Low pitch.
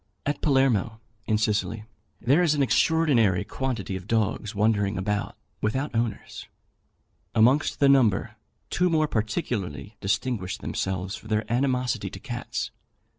Yes: low, 110 Hz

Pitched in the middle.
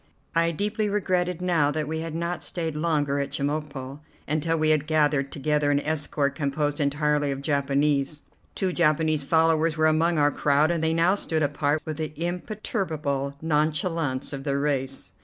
Yes: medium, 155 Hz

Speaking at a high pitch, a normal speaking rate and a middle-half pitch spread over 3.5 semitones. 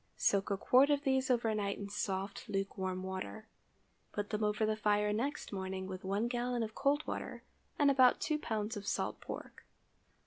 Yes: high, 210 Hz; average, 180 wpm; average, 3.9 semitones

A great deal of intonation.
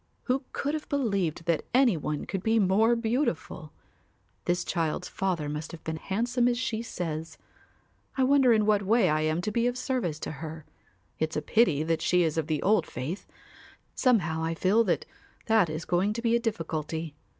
Yes: wide, 6.4 semitones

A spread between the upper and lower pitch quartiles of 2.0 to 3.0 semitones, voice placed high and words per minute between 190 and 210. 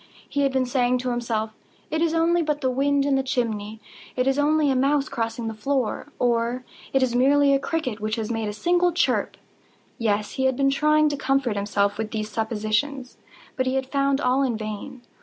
No: average, 3.9 semitones; very high, 255 Hz; average, 200 wpm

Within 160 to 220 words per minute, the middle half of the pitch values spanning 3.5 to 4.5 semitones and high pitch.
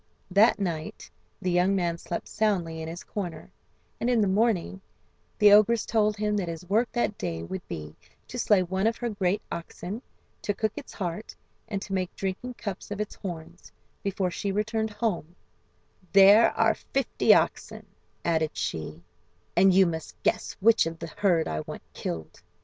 Yes: average, 170 wpm; average, 3.9 semitones; high, 195 Hz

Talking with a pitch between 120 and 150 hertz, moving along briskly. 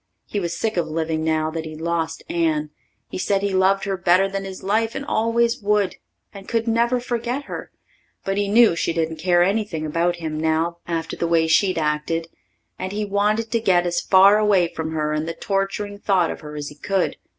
No: medium, 185 Hz; fast, 210 wpm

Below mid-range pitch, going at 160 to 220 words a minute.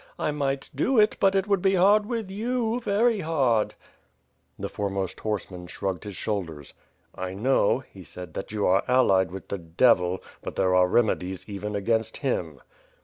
Yes: low, 110 Hz; average, 170 wpm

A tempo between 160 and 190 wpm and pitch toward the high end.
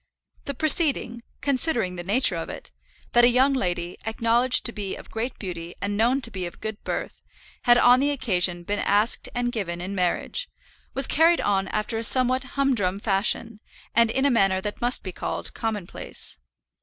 Yes: average, 180 wpm; high, 225 Hz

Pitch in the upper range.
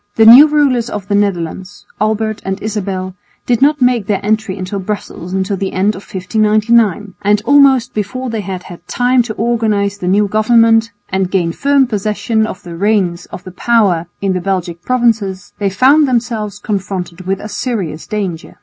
Yes: high, 210 Hz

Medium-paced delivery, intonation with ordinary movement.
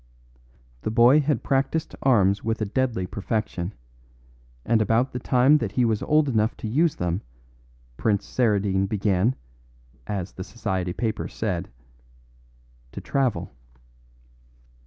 No: slow, 125 wpm; average, 4.3 semitones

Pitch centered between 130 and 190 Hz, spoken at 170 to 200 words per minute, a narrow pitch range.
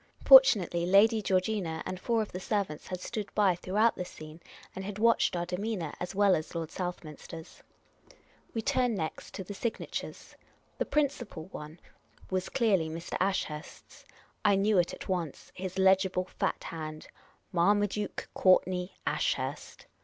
No: medium, 185 Hz; average, 175 wpm; average, 3.2 semitones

